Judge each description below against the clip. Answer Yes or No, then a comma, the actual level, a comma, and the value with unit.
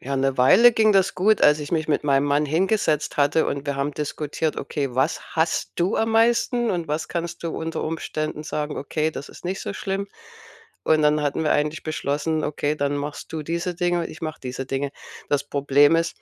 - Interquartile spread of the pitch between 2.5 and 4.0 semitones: Yes, average, 2.9 semitones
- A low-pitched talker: No, medium, 155 Hz